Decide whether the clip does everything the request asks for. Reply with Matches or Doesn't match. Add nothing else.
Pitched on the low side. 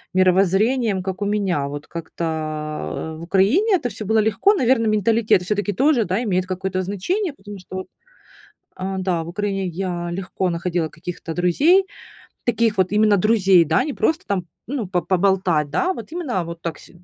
Doesn't match